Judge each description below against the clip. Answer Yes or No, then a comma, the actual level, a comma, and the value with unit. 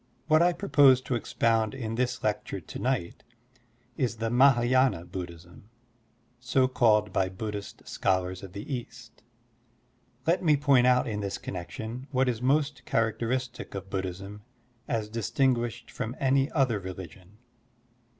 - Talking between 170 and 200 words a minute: No, average, 140 wpm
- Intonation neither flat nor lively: Yes, average, 4.4 semitones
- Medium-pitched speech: No, low, 115 Hz